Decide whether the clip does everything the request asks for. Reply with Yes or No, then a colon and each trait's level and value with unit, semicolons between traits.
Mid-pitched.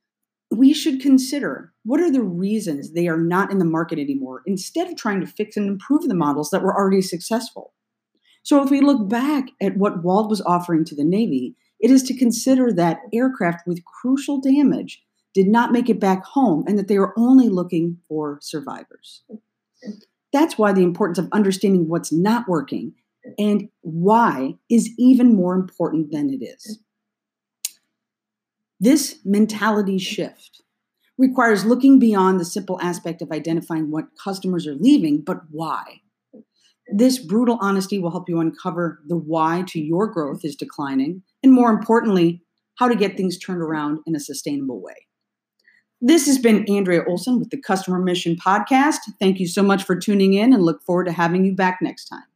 No: high, 200 Hz